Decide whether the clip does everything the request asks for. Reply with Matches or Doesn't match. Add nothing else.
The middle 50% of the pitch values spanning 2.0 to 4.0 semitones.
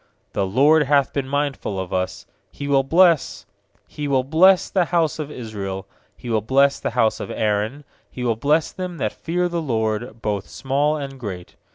Doesn't match